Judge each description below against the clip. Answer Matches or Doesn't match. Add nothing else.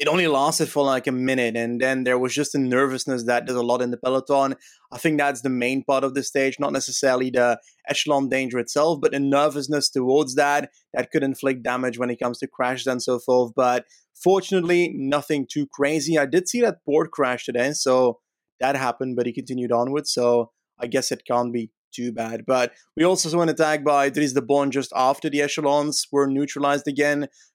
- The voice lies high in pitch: Doesn't match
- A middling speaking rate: Doesn't match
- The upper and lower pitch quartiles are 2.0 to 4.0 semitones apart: Matches